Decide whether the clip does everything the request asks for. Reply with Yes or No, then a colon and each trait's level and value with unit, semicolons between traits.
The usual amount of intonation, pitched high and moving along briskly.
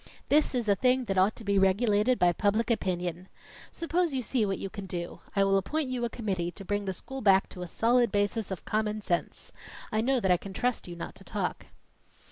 Yes: average, 4.2 semitones; high, 205 Hz; fast, 230 wpm